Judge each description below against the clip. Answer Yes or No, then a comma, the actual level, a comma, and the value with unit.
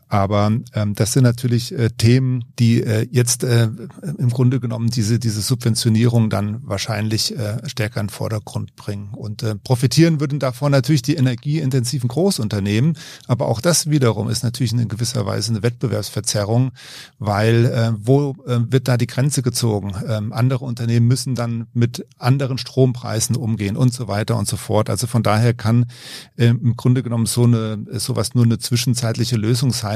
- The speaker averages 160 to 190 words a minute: Yes, average, 170 wpm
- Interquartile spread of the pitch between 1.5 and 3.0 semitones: Yes, narrow, 2.6 semitones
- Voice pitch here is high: No, low, 120 Hz